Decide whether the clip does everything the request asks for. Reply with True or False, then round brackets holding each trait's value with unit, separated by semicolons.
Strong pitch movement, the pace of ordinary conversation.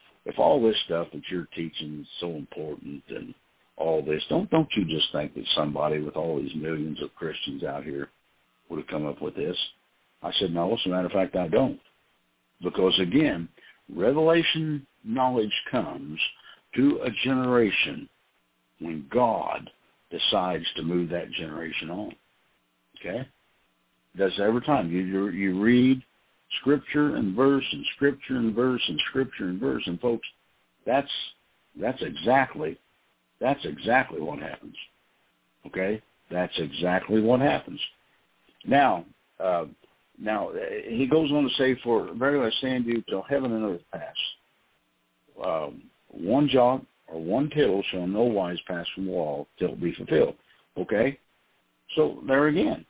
True (8.5 semitones; 150 wpm)